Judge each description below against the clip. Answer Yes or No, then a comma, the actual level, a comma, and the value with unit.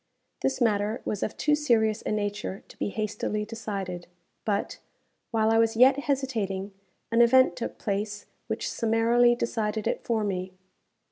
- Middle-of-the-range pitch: No, high, 220 Hz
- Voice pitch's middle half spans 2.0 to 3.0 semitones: Yes, narrow, 2.5 semitones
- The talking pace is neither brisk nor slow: Yes, average, 150 wpm